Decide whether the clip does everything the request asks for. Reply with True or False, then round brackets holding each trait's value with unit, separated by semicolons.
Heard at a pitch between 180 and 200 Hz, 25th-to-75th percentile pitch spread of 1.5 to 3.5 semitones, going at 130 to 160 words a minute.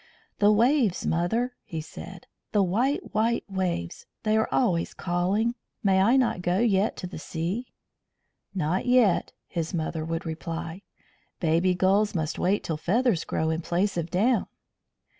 False (185 Hz; 4.5 semitones; 150 wpm)